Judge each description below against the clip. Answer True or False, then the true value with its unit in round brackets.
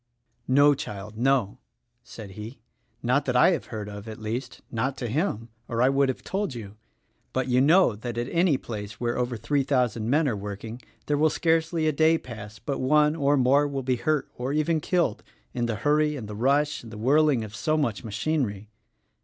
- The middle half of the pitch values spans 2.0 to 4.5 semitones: False (4.9 semitones)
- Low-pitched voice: True (130 Hz)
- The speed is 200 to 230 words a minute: True (205 wpm)